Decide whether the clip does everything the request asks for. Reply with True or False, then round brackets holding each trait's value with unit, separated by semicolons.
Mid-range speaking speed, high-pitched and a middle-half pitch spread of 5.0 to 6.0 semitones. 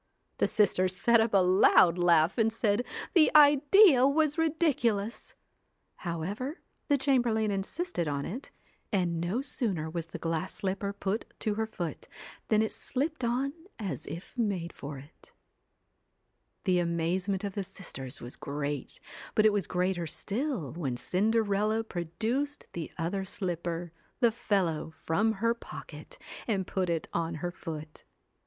True (150 wpm; 195 Hz; 5.5 semitones)